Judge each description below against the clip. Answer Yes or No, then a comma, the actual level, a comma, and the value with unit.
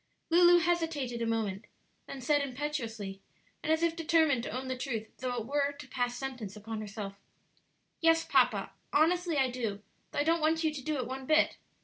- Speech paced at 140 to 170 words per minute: No, average, 195 wpm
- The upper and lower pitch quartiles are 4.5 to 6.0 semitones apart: Yes, wide, 5.4 semitones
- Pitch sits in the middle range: No, very high, 270 Hz